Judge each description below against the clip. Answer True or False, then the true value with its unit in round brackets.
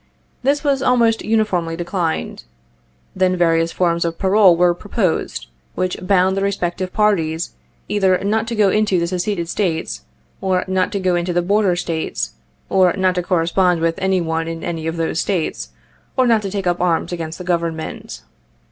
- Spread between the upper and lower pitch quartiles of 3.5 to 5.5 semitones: False (2.9 semitones)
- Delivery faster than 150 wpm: True (175 wpm)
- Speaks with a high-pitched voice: False (180 Hz)